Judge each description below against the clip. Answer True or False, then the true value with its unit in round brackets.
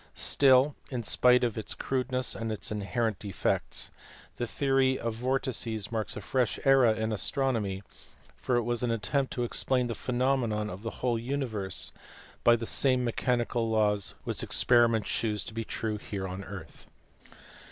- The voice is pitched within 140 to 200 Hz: False (115 Hz)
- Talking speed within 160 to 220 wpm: True (165 wpm)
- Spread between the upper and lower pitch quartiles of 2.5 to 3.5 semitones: True (2.8 semitones)